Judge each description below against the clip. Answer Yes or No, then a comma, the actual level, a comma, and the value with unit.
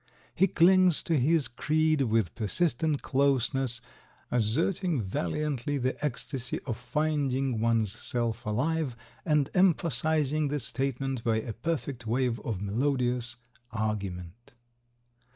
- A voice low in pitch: Yes, low, 130 Hz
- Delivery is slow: Yes, slow, 110 wpm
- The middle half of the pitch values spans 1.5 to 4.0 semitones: No, average, 4.8 semitones